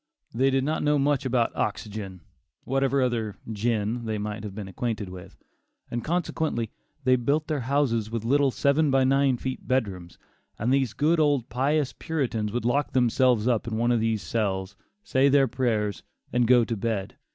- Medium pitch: No, low, 120 Hz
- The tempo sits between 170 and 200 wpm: Yes, average, 175 wpm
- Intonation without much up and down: No, average, 3.9 semitones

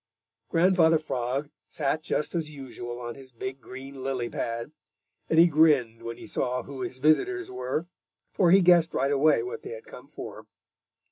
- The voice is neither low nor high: Yes, medium, 145 Hz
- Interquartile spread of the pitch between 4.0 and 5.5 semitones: Yes, average, 4.7 semitones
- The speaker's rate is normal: Yes, average, 175 wpm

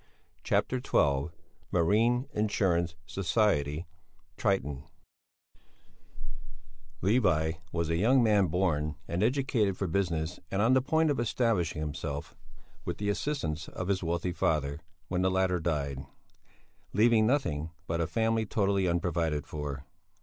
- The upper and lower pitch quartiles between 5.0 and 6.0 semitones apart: Yes, wide, 5.4 semitones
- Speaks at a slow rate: Yes, slow, 125 wpm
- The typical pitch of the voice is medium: No, very low, 90 Hz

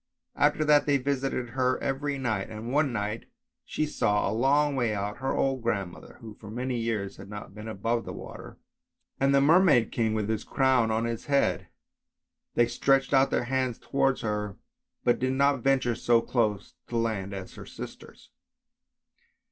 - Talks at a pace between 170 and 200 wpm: Yes, average, 175 wpm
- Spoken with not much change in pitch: No, average, 3.8 semitones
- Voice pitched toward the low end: Yes, low, 120 Hz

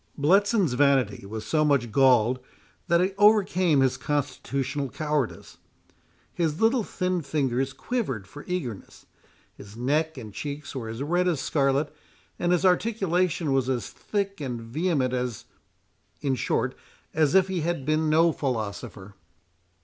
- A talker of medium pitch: Yes, medium, 145 Hz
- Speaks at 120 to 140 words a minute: Yes, slow, 135 wpm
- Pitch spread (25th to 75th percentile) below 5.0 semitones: No, wide, 5.4 semitones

